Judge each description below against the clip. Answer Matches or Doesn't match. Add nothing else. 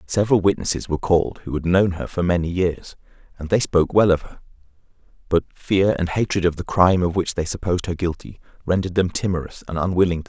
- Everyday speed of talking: Doesn't match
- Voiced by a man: Matches